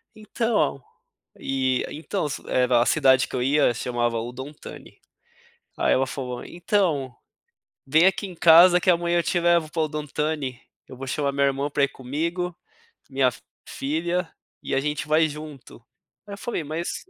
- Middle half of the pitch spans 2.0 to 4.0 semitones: No, average, 4.4 semitones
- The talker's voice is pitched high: No, medium, 150 Hz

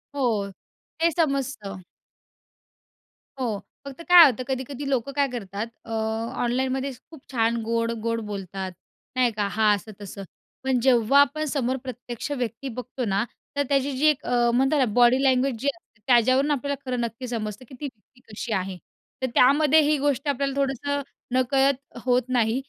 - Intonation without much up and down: No, average, 3.2 semitones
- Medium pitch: No, very high, 255 Hz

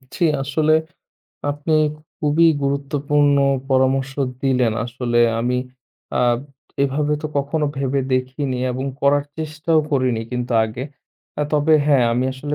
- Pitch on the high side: No, medium, 140 Hz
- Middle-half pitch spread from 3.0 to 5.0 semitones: No, narrow, 2.4 semitones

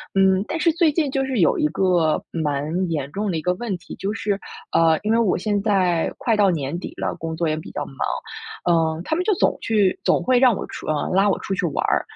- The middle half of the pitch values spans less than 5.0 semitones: No, wide, 5.5 semitones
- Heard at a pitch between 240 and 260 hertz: No, high, 190 Hz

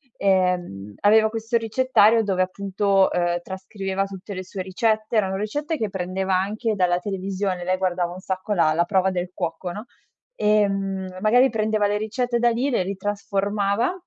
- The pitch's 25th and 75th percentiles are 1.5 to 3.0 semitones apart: Yes, narrow, 2.6 semitones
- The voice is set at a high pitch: Yes, high, 195 Hz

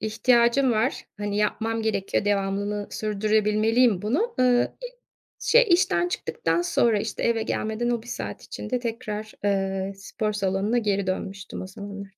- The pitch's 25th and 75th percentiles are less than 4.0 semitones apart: Yes, average, 2.9 semitones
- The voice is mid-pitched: No, high, 215 Hz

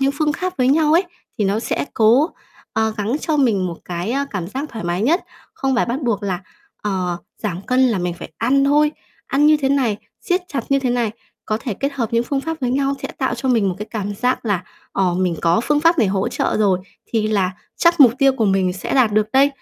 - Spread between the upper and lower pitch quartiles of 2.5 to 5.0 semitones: No, wide, 5.6 semitones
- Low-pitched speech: No, high, 235 Hz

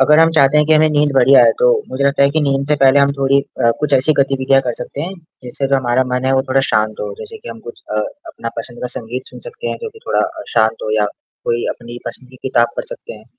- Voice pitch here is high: No, low, 135 Hz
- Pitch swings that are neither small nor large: Yes, average, 3.6 semitones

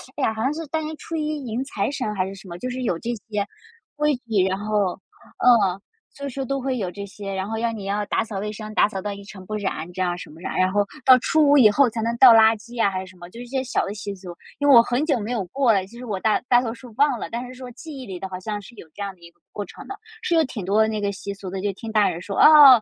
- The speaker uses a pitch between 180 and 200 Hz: No, high, 220 Hz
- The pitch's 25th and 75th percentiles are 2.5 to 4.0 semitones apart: No, average, 4.4 semitones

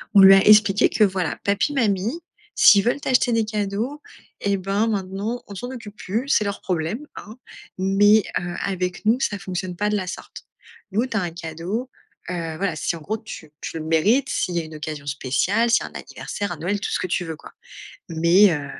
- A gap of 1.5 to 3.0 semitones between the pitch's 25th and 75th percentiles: No, average, 3.7 semitones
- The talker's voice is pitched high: Yes, high, 195 Hz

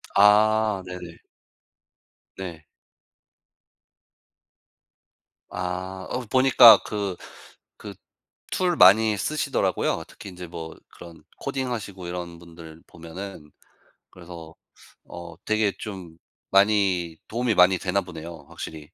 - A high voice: No, very low, 95 Hz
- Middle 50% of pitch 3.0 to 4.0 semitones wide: Yes, average, 3.6 semitones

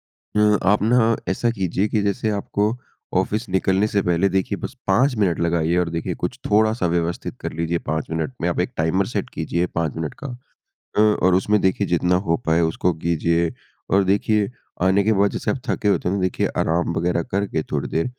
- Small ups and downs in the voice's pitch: No, average, 3.6 semitones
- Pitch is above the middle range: No, very low, 95 Hz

